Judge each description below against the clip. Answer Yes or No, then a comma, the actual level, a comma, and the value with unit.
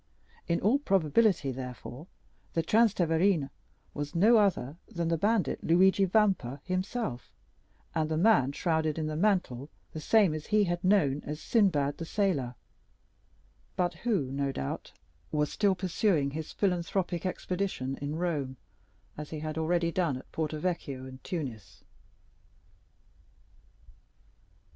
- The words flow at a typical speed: No, slow, 130 wpm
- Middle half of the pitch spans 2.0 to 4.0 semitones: No, average, 4.8 semitones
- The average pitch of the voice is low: No, medium, 165 Hz